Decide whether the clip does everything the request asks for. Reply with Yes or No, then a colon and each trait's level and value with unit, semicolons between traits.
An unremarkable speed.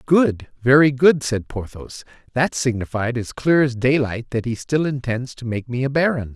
Yes: average, 190 wpm